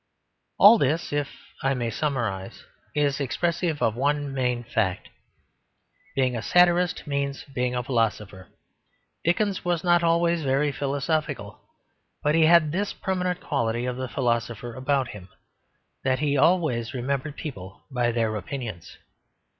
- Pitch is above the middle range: No, low, 135 Hz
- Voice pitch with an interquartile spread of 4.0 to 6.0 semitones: Yes, average, 4.9 semitones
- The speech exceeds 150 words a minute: No, slow, 135 wpm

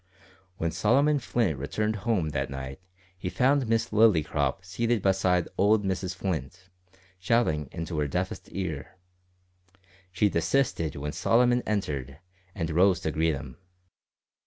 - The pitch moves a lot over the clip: Yes, wide, 5.8 semitones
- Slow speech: Yes, slow, 130 wpm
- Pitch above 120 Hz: No, very low, 90 Hz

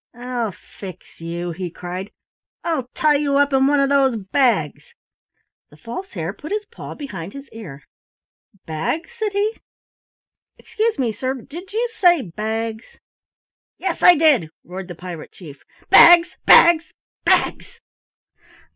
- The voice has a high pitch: Yes, very high, 250 Hz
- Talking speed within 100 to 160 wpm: Yes, average, 140 wpm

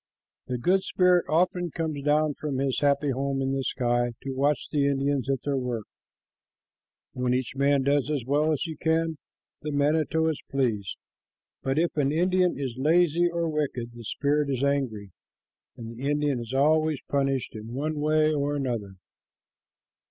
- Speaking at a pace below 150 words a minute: No, average, 165 wpm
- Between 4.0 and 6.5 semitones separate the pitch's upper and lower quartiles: No, average, 2.9 semitones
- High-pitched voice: No, medium, 140 Hz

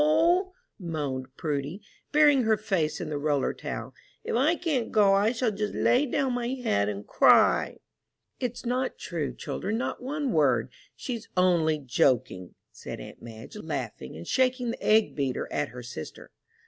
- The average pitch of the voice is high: Yes, high, 195 Hz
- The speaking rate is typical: Yes, average, 160 wpm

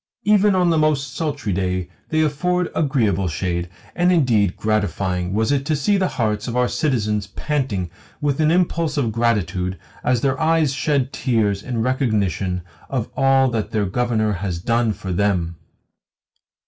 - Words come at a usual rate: Yes, average, 160 wpm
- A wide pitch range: Yes, wide, 6.6 semitones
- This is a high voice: No, low, 120 Hz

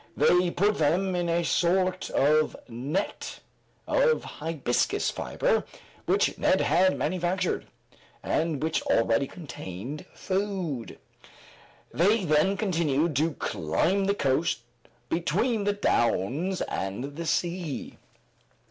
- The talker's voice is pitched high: No, medium, 170 Hz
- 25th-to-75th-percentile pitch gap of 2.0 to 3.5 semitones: No, average, 4.6 semitones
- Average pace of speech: No, slow, 105 wpm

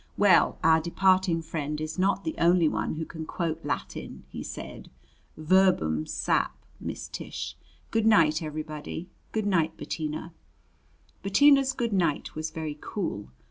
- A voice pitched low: No, medium, 165 Hz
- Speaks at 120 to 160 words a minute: Yes, average, 140 wpm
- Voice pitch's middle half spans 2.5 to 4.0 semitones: Yes, average, 3.5 semitones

